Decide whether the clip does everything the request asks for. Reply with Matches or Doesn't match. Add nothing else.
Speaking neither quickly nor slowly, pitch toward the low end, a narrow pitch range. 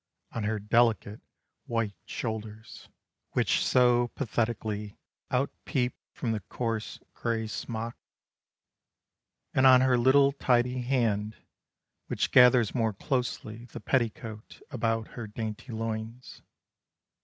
Doesn't match